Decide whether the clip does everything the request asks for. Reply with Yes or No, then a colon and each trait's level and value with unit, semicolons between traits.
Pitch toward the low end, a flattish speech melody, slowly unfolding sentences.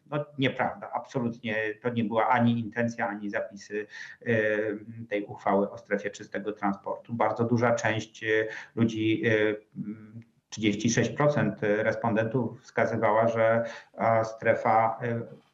Yes: low, 115 Hz; narrow, 1.6 semitones; slow, 95 wpm